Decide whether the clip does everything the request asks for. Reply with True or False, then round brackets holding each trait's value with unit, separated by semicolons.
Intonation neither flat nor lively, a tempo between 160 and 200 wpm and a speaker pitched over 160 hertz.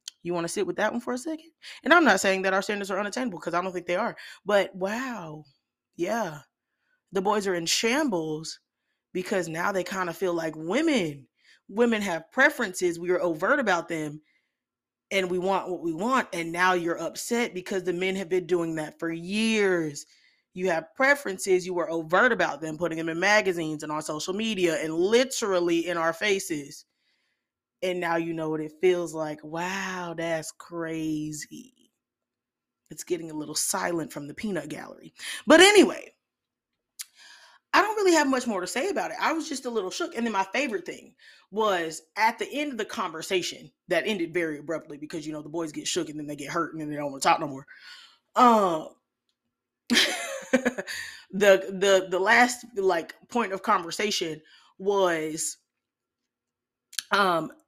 True (4.4 semitones; 180 wpm; 185 Hz)